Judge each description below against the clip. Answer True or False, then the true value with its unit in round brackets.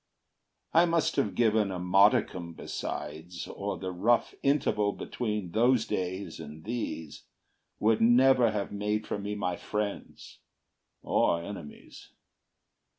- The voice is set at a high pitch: False (105 Hz)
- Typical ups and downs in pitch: True (4.0 semitones)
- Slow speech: True (120 wpm)